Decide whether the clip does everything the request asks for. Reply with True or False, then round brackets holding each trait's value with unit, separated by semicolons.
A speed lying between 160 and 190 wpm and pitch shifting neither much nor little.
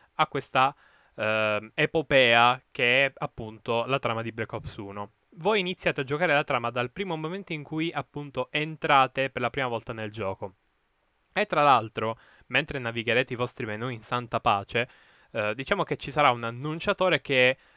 True (170 wpm; 4.3 semitones)